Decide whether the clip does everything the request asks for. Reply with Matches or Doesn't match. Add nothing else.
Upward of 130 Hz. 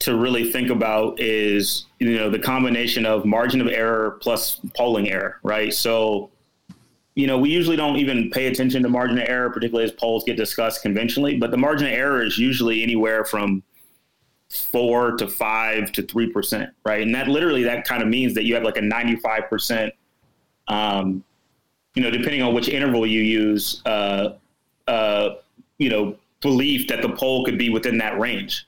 Doesn't match